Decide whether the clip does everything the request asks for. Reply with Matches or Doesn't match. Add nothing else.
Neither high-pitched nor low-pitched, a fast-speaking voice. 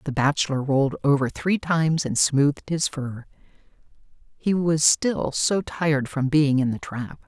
Doesn't match